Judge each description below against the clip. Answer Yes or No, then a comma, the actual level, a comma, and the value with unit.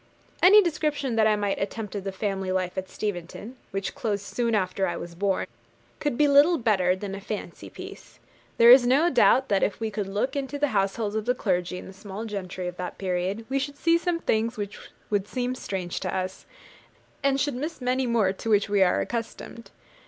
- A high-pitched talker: Yes, high, 215 Hz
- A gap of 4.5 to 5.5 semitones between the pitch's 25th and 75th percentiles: Yes, average, 4.9 semitones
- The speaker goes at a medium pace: No, fast, 210 wpm